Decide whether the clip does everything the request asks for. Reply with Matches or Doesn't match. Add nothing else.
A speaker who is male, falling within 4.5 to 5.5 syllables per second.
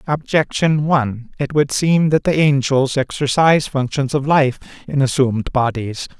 Matches